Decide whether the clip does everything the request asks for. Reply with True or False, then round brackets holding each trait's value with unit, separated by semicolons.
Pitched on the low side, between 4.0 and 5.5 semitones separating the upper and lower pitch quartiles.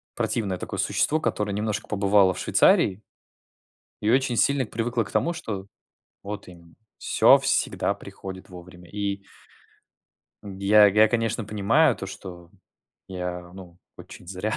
False (100 Hz; 2.9 semitones)